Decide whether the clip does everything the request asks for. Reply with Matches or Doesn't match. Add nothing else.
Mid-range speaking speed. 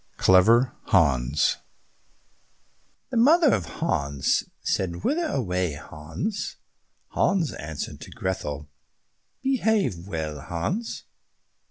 Doesn't match